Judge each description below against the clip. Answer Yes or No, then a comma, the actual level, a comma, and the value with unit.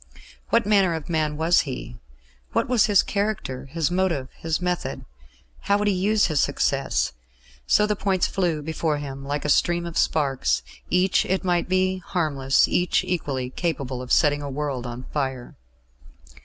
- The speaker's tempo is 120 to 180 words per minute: Yes, average, 165 wpm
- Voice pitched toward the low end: No, medium, 160 Hz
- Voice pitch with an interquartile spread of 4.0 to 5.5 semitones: Yes, average, 5.0 semitones